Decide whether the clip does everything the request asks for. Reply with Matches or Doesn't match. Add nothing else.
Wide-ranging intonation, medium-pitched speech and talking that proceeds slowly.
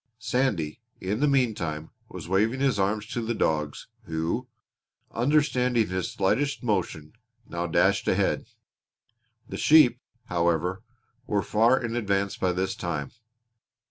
Doesn't match